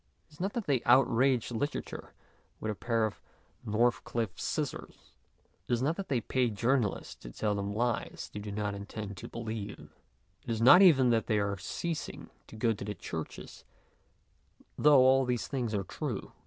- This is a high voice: No, low, 115 Hz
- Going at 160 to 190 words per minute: Yes, average, 185 wpm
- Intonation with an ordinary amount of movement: Yes, average, 3.9 semitones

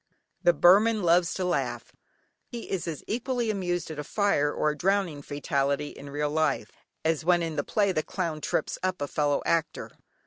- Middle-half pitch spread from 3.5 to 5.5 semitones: Yes, average, 4.4 semitones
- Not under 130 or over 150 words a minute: No, average, 185 wpm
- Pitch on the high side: No, medium, 170 Hz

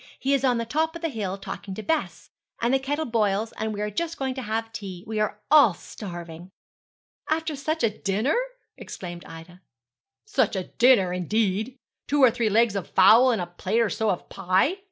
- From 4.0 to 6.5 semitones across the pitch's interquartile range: Yes, wide, 5.4 semitones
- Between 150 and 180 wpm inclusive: No, average, 200 wpm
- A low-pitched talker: No, high, 220 Hz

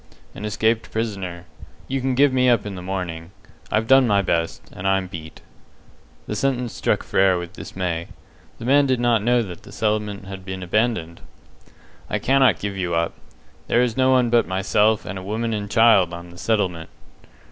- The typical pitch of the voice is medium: No, low, 105 Hz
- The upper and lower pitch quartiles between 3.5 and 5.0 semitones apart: Yes, average, 4.4 semitones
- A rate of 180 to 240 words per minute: Yes, average, 185 wpm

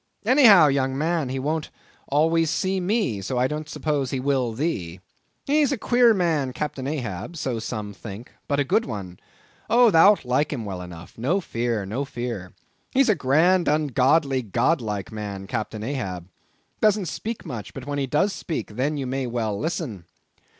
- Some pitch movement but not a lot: No, wide, 6.6 semitones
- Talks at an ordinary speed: Yes, average, 170 wpm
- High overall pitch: No, low, 135 Hz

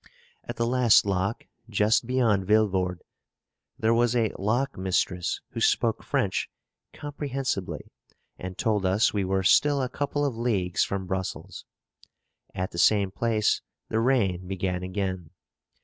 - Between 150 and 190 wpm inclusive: No, slow, 135 wpm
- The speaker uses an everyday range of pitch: Yes, average, 4.2 semitones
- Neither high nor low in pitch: No, low, 105 Hz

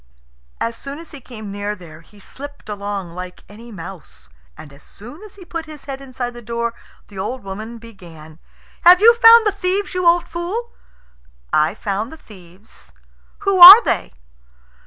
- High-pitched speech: Yes, high, 235 Hz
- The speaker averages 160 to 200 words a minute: Yes, average, 175 wpm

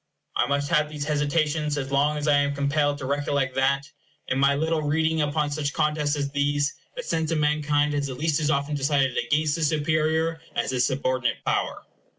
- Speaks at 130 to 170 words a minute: No, average, 195 wpm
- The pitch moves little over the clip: Yes, narrow, 1.4 semitones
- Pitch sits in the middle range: Yes, medium, 145 Hz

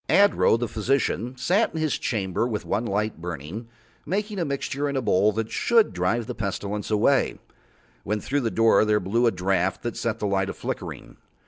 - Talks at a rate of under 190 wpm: No, average, 195 wpm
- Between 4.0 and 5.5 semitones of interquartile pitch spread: Yes, average, 5.0 semitones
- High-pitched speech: No, low, 115 Hz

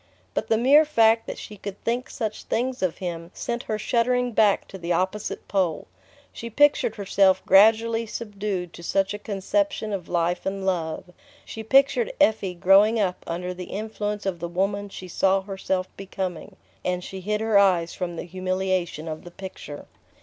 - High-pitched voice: Yes, high, 195 Hz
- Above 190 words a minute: No, average, 175 wpm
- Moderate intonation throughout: Yes, average, 3.3 semitones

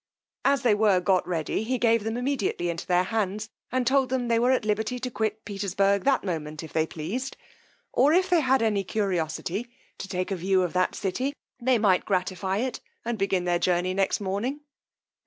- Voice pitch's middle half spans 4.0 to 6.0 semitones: Yes, average, 5.0 semitones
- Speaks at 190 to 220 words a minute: Yes, average, 195 wpm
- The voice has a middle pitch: No, high, 205 Hz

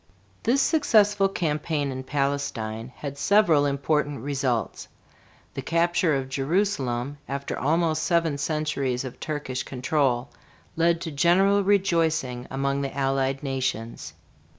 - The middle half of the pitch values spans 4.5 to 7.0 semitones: No, average, 3.9 semitones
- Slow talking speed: Yes, slow, 115 wpm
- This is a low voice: No, medium, 145 Hz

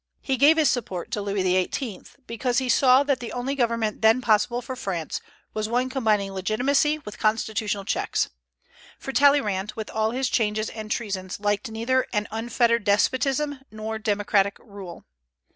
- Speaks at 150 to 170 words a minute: Yes, average, 160 wpm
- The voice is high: Yes, high, 220 Hz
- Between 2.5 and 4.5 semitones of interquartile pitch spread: Yes, average, 3.6 semitones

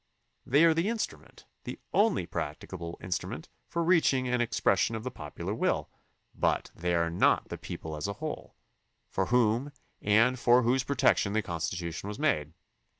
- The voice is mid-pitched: No, low, 115 Hz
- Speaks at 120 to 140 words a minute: No, average, 165 wpm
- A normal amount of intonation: No, wide, 8.0 semitones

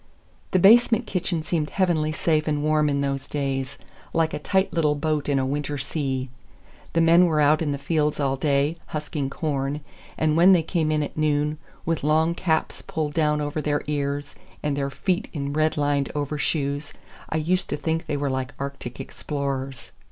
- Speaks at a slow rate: No, average, 180 wpm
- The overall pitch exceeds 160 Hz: No, medium, 150 Hz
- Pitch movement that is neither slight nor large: No, narrow, 2.1 semitones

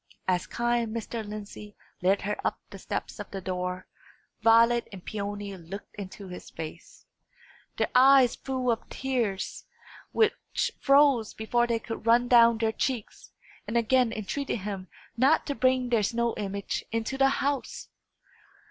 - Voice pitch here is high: Yes, high, 230 Hz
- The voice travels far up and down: No, average, 3.6 semitones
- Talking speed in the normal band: Yes, average, 150 wpm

